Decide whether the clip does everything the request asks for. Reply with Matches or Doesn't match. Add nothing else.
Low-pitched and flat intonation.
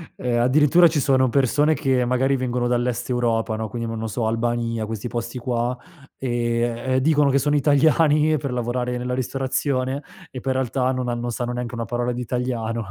Matches